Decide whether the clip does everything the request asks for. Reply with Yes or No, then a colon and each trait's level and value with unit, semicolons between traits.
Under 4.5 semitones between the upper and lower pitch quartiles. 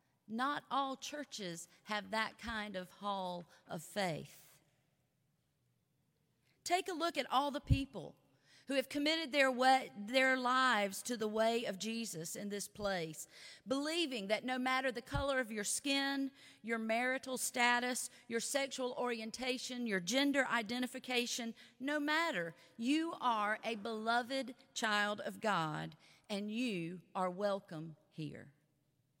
No: average, 5.1 semitones